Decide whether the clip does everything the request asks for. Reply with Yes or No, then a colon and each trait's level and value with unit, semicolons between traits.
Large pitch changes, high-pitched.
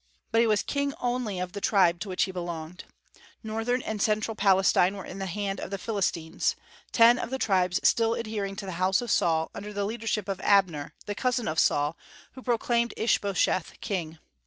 No: average, 3.6 semitones; high, 200 Hz